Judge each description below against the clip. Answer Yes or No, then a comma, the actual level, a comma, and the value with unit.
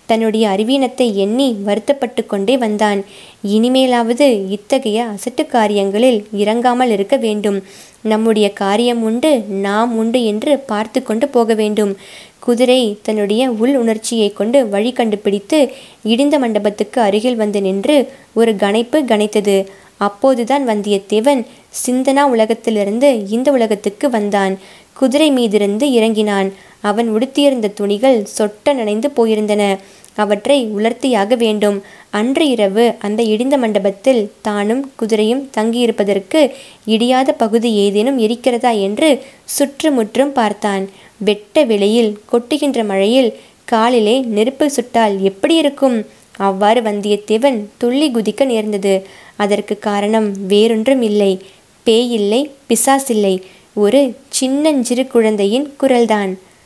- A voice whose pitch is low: No, high, 225 Hz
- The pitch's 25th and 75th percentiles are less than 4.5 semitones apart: Yes, average, 3.8 semitones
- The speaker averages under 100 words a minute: No, average, 105 wpm